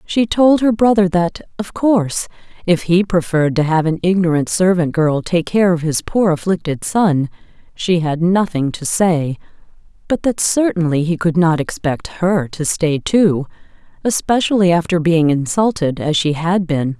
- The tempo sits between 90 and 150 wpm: No, average, 165 wpm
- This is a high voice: No, medium, 175 Hz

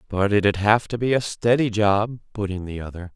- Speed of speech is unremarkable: No, fast, 230 wpm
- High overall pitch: No, low, 105 Hz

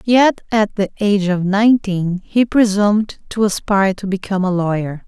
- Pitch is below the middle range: No, high, 200 Hz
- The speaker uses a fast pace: No, average, 165 wpm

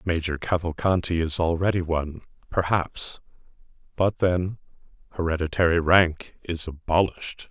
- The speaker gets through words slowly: Yes, slow, 95 wpm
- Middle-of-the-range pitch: No, very low, 85 Hz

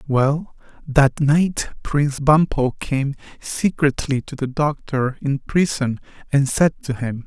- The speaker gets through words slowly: Yes, slow, 130 wpm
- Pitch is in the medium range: Yes, medium, 145 Hz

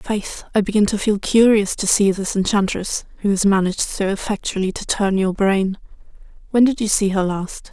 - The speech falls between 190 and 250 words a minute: Yes, average, 195 wpm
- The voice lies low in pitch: No, high, 200 Hz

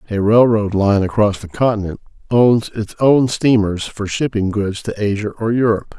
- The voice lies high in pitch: No, low, 105 Hz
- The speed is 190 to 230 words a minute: No, average, 170 wpm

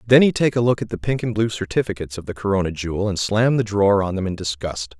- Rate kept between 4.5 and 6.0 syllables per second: No, 6.5 syllables/s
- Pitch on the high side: No, low, 100 Hz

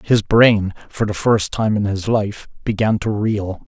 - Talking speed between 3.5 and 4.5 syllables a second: Yes, 4.0 syllables/s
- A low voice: Yes, low, 105 Hz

